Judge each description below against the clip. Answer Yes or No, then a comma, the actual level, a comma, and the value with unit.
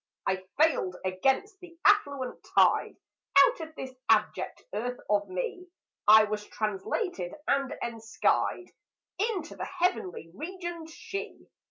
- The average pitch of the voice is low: No, very high, 270 Hz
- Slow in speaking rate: Yes, slow, 120 wpm